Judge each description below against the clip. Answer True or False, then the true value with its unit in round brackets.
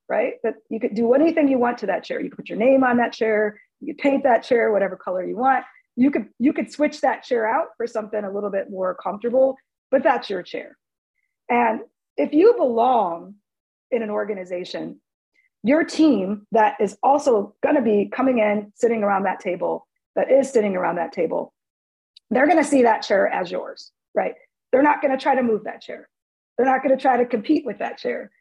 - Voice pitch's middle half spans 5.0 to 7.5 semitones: True (5.3 semitones)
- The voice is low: False (245 Hz)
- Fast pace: True (210 wpm)